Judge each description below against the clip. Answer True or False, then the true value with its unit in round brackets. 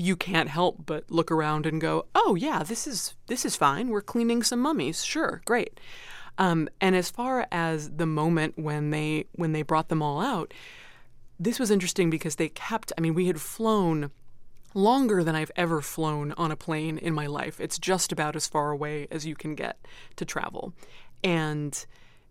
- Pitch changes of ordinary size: True (4.0 semitones)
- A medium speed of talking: True (190 wpm)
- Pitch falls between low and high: True (165 Hz)